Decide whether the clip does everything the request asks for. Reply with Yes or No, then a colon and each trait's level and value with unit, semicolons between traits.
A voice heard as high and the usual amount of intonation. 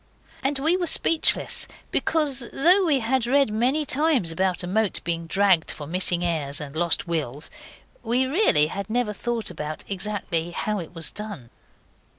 No: high, 210 Hz; wide, 7.8 semitones